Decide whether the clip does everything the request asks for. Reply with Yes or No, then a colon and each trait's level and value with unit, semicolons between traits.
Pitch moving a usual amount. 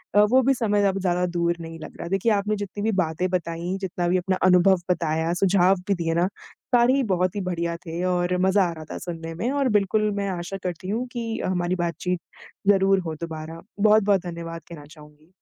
Yes: average, 3.0 semitones